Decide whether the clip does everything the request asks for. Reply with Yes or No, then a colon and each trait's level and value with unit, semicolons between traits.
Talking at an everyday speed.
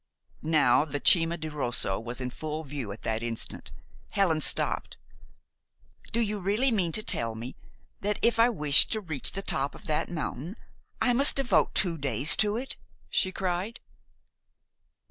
Yes: average, 165 wpm